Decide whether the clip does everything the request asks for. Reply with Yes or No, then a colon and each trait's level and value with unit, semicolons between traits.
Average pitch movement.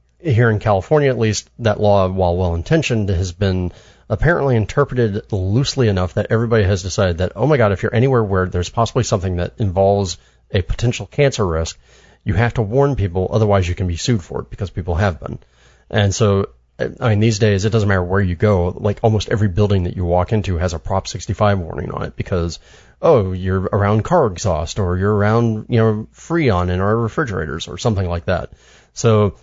Yes: average, 3.6 semitones